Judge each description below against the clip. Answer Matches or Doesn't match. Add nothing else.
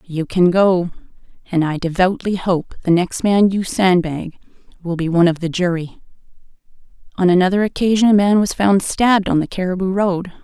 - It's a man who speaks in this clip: Doesn't match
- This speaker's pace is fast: Doesn't match